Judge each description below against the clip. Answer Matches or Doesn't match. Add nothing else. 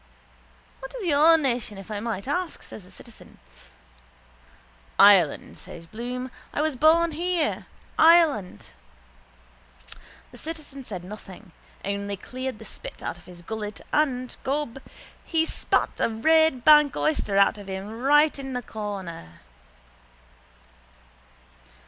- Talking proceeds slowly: Matches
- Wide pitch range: Matches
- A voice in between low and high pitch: Doesn't match